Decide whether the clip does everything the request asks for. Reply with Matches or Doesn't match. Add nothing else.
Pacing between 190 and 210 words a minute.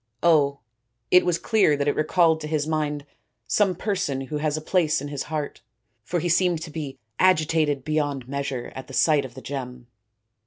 Matches